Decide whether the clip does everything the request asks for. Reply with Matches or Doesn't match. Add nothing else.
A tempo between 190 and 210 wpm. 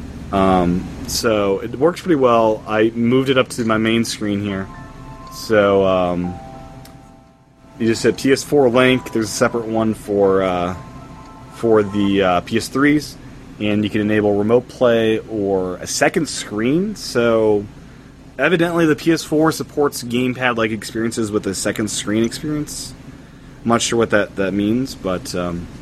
Doesn't match